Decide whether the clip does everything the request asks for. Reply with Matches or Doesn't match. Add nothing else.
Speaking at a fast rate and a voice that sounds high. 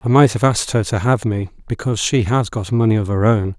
Doesn't match